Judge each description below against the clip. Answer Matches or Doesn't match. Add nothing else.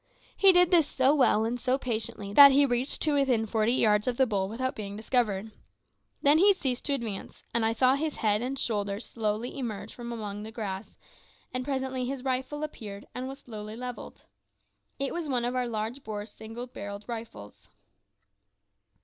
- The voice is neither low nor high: Doesn't match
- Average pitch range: Matches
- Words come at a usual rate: Matches